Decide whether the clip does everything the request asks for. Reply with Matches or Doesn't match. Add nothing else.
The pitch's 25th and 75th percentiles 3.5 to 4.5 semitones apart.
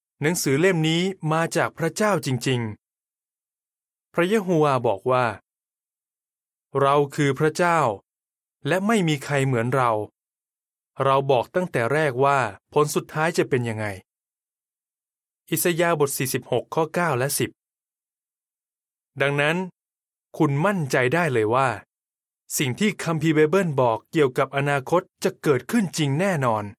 Matches